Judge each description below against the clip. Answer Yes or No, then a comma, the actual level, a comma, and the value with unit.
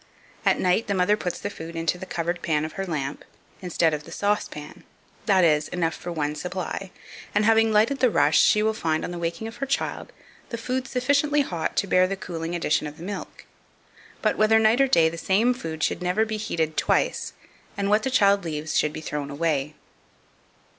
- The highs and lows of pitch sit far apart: No, average, 5.0 semitones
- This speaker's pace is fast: Yes, fast, 210 wpm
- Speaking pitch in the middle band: Yes, medium, 180 Hz